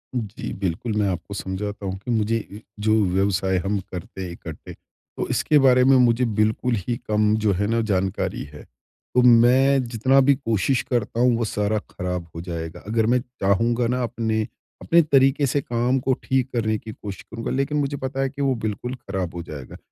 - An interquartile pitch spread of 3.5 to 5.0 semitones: Yes, average, 4.2 semitones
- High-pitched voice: No, low, 115 Hz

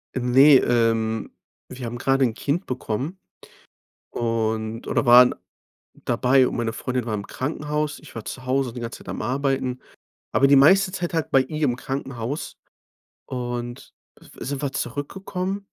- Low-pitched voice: Yes, low, 130 Hz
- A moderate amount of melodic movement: Yes, average, 3.1 semitones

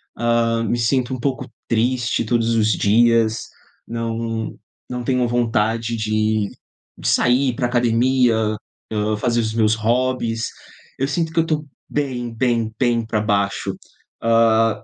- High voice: No, low, 115 Hz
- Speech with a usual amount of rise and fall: No, narrow, 1.7 semitones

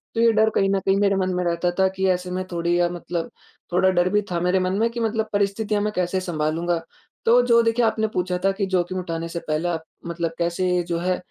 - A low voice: No, medium, 185 Hz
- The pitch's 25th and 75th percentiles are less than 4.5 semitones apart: Yes, average, 2.7 semitones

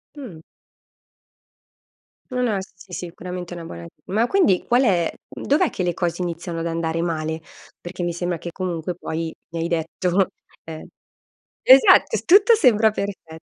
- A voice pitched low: No, medium, 175 Hz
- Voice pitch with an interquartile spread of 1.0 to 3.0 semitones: No, average, 3.5 semitones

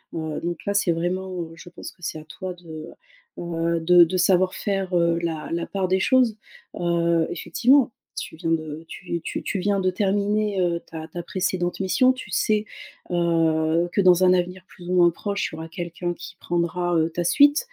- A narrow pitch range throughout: Yes, narrow, 2.1 semitones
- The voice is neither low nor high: Yes, medium, 175 Hz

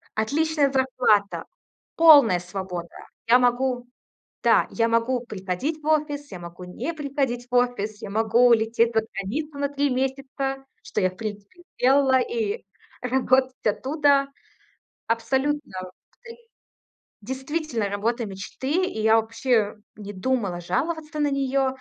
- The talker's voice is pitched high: Yes, very high, 250 Hz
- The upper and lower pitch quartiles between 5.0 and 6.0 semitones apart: No, average, 4.6 semitones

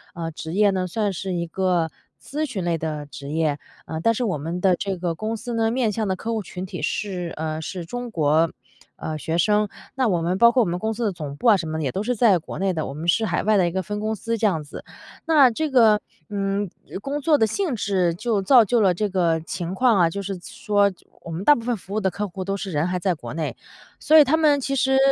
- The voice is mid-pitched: No, high, 195 Hz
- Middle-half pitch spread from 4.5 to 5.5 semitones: Yes, average, 4.8 semitones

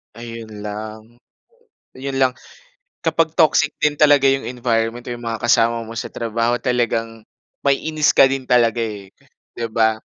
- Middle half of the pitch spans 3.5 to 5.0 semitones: No, average, 3.1 semitones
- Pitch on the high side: No, low, 120 Hz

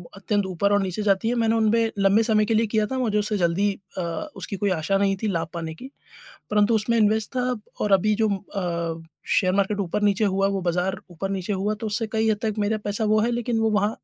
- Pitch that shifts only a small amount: Yes, narrow, 2.3 semitones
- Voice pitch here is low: No, high, 205 Hz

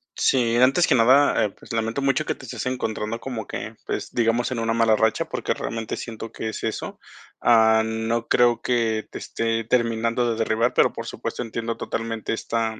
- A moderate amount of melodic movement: No, narrow, 1.3 semitones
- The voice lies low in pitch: Yes, low, 115 Hz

